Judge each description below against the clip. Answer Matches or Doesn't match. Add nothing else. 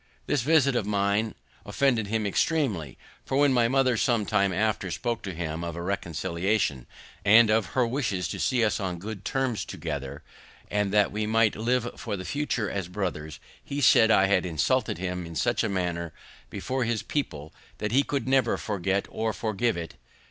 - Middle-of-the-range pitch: Doesn't match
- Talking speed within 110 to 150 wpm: Doesn't match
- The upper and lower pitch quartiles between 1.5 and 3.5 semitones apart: Doesn't match